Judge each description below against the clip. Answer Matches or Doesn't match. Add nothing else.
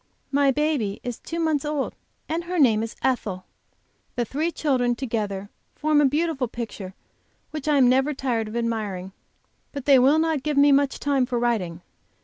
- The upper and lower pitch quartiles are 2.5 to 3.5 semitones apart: Doesn't match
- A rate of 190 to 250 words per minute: Doesn't match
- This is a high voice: Matches